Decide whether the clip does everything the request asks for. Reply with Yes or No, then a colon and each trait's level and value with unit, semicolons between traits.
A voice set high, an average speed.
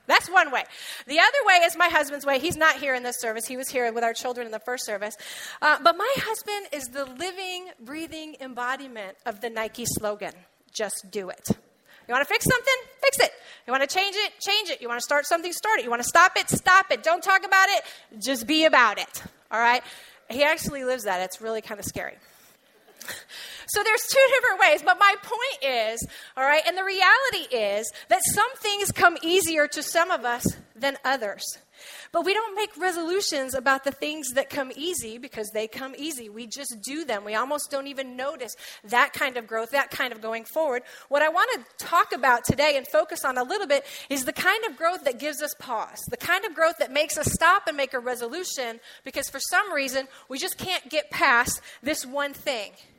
No: very high, 285 Hz; fast, 220 wpm